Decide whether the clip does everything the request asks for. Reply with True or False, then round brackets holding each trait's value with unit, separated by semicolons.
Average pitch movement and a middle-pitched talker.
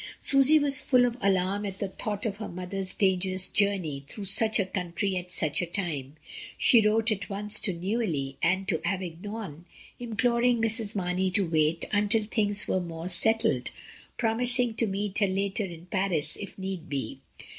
False (3.5 semitones; 195 Hz)